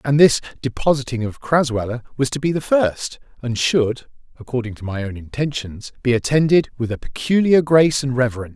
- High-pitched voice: No, low, 130 Hz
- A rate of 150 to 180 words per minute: Yes, average, 160 wpm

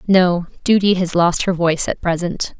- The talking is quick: No, average, 185 wpm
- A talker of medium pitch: Yes, medium, 180 Hz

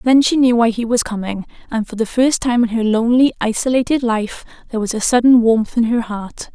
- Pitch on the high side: Yes, high, 235 Hz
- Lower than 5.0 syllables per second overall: No, 5.6 syllables/s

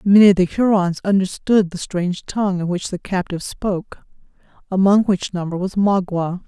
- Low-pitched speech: No, high, 190 Hz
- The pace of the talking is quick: No, average, 165 wpm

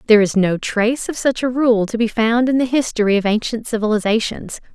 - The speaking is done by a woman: Yes, female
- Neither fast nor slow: No, fast, 215 wpm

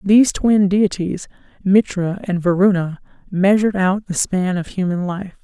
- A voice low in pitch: No, high, 190 Hz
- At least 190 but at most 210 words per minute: No, average, 145 wpm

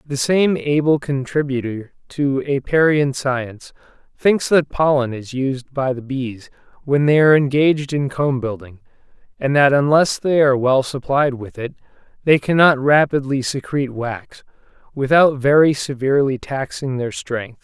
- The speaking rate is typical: Yes, average, 145 wpm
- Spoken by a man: Yes, male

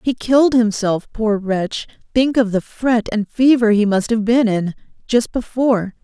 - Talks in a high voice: Yes, high, 225 Hz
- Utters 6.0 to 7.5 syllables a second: No, 4.4 syllables/s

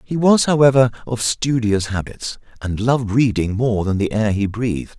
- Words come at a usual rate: Yes, average, 180 wpm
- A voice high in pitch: No, low, 115 Hz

